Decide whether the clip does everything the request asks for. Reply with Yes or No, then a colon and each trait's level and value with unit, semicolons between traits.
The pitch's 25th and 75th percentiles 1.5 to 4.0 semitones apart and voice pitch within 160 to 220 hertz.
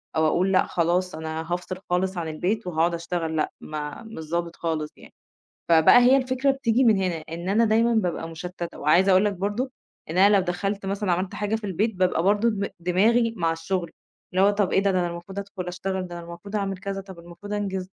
Yes: average, 3.1 semitones; medium, 185 Hz